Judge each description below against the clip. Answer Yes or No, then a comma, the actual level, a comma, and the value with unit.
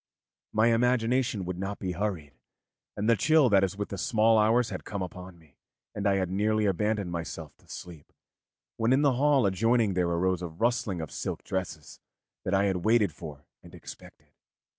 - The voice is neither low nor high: No, low, 100 Hz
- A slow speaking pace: No, average, 185 wpm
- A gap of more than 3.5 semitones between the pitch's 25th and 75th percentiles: Yes, average, 4.2 semitones